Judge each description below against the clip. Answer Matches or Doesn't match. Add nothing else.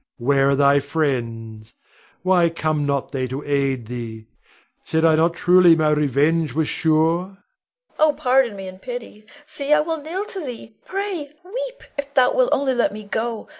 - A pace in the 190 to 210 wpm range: Doesn't match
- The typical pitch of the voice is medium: Matches